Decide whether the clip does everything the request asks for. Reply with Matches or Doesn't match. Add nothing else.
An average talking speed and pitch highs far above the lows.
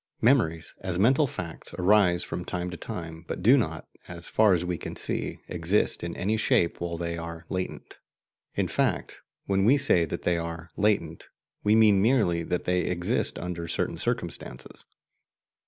Doesn't match